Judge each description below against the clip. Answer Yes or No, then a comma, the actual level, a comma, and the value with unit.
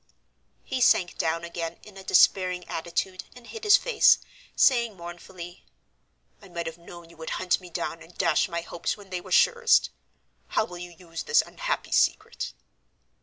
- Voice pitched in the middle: Yes, medium, 180 Hz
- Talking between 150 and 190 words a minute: Yes, average, 170 wpm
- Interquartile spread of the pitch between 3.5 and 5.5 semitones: Yes, average, 3.8 semitones